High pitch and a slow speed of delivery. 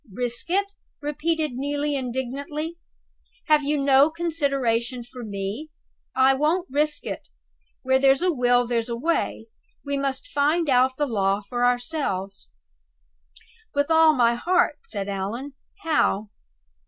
Yes: very high, 270 Hz; slow, 130 wpm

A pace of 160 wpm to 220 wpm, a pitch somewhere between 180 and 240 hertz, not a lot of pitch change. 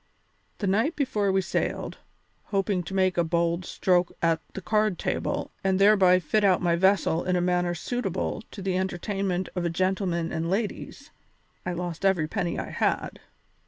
Yes: average, 170 wpm; medium, 185 Hz; narrow, 2.1 semitones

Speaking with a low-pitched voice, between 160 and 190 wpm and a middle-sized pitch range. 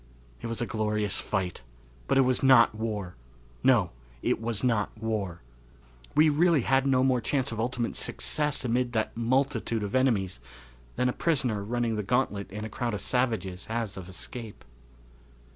Yes: low, 115 Hz; average, 165 wpm; average, 3.4 semitones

